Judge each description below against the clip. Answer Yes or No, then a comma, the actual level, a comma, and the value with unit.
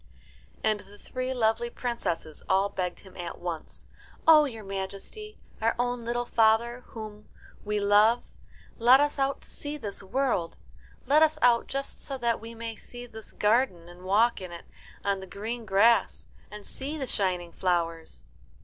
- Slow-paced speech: No, average, 165 wpm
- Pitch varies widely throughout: No, average, 4.1 semitones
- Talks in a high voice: Yes, high, 220 Hz